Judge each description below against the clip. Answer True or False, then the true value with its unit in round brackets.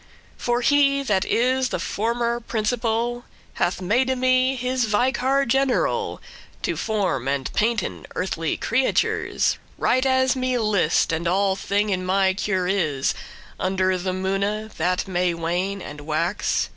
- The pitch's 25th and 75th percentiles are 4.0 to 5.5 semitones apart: True (5.2 semitones)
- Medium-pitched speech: False (210 Hz)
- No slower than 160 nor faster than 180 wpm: False (140 wpm)